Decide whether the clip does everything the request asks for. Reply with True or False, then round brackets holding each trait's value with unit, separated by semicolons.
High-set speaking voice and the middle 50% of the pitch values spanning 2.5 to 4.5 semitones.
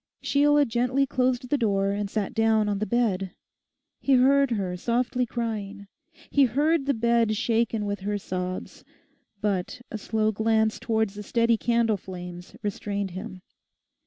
True (220 Hz; 3.3 semitones)